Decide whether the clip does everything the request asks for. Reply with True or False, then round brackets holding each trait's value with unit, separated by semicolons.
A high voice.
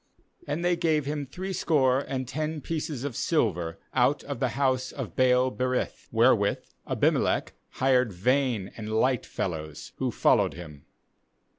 False (130 Hz)